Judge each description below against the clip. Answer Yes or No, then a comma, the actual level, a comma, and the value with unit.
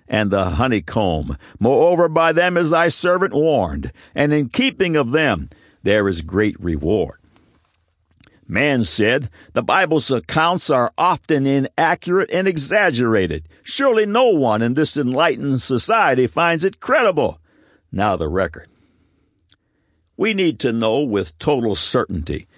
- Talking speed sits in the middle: No, slow, 130 wpm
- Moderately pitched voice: Yes, medium, 145 Hz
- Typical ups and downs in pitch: No, wide, 8.0 semitones